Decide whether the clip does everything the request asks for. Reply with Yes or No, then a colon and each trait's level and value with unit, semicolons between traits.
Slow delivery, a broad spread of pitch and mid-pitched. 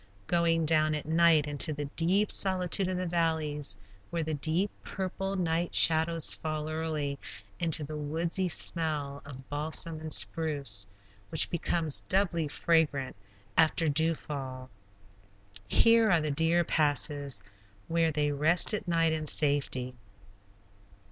No: slow, 130 wpm; narrow, 2.4 semitones; medium, 160 Hz